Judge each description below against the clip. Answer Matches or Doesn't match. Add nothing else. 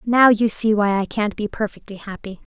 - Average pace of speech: Doesn't match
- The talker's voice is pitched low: Doesn't match